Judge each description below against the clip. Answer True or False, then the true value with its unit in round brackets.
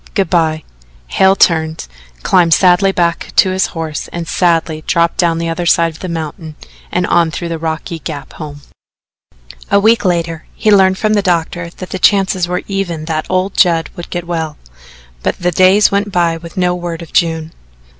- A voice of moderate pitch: True (170 Hz)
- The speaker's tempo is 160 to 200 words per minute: True (185 wpm)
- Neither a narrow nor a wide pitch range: False (2.2 semitones)